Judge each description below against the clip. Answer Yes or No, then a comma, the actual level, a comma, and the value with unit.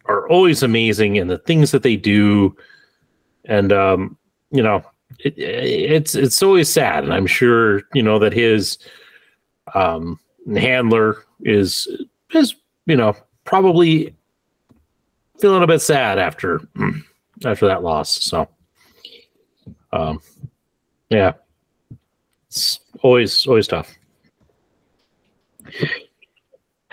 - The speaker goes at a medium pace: No, slow, 105 wpm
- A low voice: Yes, low, 125 Hz